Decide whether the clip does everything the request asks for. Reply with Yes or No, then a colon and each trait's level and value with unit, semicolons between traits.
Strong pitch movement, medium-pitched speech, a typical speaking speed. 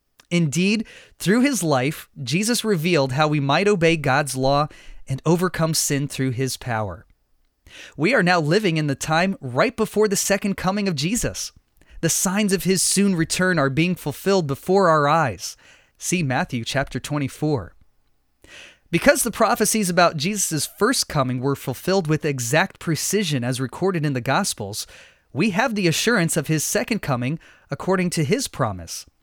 Yes: wide, 5.9 semitones; medium, 160 Hz; average, 160 wpm